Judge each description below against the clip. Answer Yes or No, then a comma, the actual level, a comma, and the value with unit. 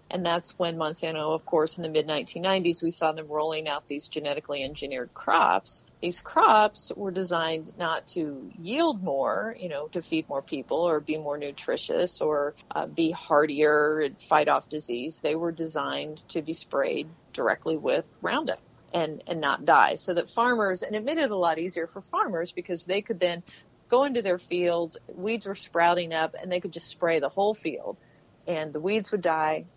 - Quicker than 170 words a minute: Yes, average, 190 wpm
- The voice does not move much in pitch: No, average, 3.6 semitones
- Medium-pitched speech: Yes, medium, 170 Hz